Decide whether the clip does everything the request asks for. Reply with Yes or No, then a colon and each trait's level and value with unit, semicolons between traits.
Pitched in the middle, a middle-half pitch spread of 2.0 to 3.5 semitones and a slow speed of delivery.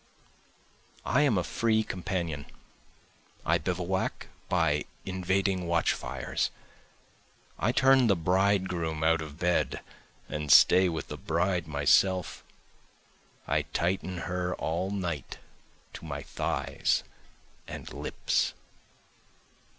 No: very low, 90 Hz; narrow, 2.6 semitones; slow, 100 wpm